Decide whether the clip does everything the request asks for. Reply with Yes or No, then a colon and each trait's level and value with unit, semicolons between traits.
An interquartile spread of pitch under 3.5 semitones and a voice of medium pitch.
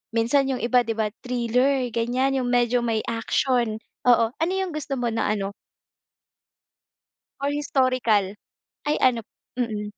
No: average, 2.8 semitones; high, 245 Hz